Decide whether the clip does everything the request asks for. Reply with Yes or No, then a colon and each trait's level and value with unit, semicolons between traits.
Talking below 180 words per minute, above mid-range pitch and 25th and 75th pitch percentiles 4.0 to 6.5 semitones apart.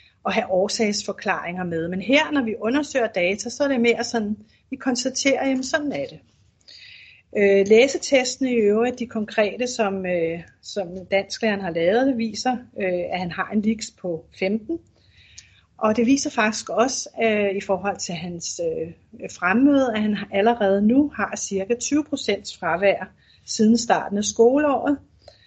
Yes: average, 150 wpm; high, 220 Hz; average, 4.7 semitones